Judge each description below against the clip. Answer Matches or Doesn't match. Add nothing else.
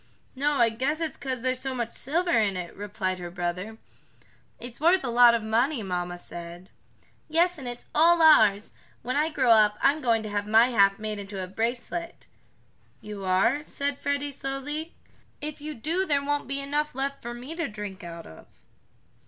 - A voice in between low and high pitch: Doesn't match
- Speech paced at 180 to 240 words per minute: Matches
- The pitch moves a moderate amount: Doesn't match